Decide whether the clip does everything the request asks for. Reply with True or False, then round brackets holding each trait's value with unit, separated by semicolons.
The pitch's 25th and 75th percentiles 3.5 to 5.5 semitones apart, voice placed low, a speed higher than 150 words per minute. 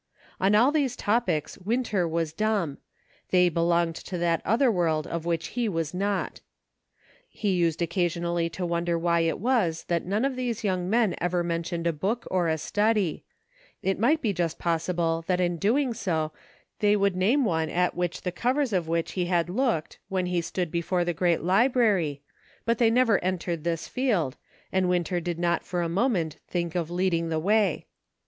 False (3.8 semitones; 180 Hz; 180 wpm)